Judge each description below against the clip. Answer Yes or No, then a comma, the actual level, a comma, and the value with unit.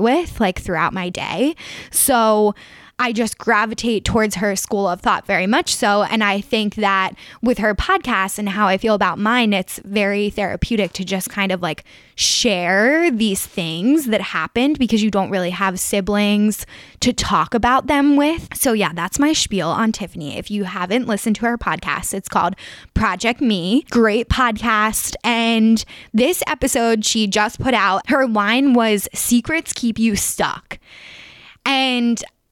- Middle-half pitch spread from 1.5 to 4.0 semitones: Yes, average, 3.4 semitones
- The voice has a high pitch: Yes, high, 220 Hz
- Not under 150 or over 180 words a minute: Yes, average, 165 wpm